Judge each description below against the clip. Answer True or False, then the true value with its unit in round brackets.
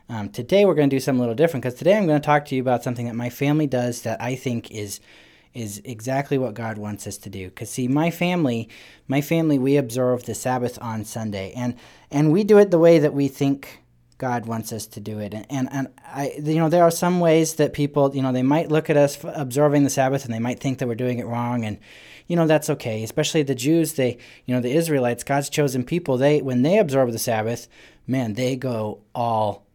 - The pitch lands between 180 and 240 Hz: False (130 Hz)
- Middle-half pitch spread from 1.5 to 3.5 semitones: False (4.0 semitones)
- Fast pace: True (245 wpm)